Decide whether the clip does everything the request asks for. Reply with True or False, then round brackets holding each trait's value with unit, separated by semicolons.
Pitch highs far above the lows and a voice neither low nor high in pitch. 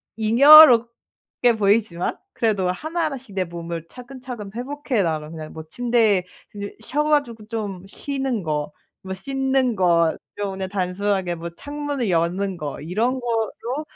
False (5.8 semitones; 215 Hz)